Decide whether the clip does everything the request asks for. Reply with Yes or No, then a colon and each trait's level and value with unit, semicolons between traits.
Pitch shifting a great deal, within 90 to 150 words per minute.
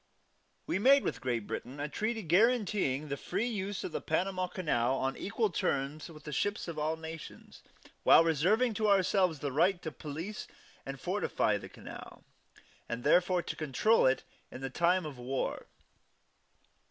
No: wide, 5.9 semitones; average, 160 wpm